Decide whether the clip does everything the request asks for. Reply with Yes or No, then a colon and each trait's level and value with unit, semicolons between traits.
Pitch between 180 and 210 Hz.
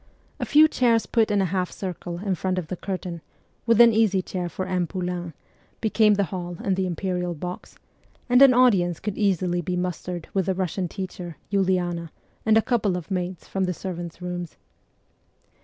Yes: medium, 185 Hz